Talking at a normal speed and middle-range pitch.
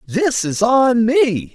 No: average, 155 wpm; high, 235 Hz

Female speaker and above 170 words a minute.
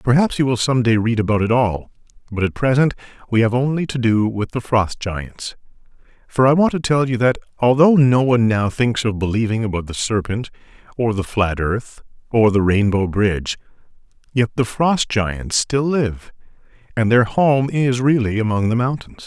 No: male; average, 185 wpm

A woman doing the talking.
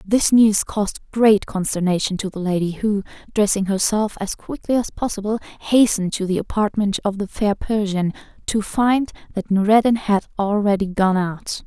Yes: female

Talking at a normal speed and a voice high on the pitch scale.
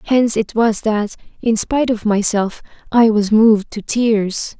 Yes: average, 170 wpm; high, 220 Hz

